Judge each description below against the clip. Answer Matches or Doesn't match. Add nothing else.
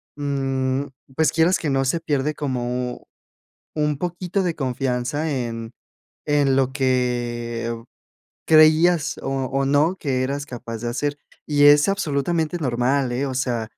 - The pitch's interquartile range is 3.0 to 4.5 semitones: Matches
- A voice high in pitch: Doesn't match